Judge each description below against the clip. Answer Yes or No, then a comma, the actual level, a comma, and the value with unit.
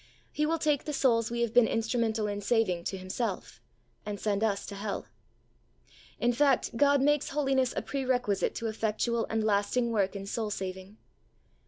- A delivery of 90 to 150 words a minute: No, average, 175 wpm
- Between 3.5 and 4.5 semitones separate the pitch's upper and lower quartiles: Yes, average, 3.9 semitones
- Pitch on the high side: Yes, high, 225 Hz